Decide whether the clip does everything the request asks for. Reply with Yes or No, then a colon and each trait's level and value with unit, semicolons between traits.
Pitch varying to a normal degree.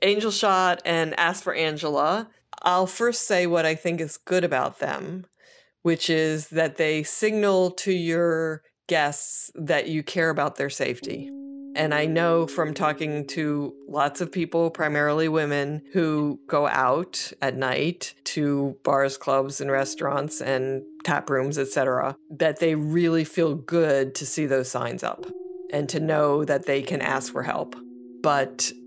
Yes: average, 3.3 semitones